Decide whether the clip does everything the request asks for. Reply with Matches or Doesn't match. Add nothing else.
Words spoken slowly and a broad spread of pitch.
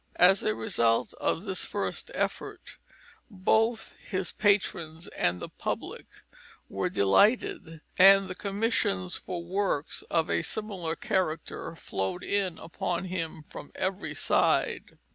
Doesn't match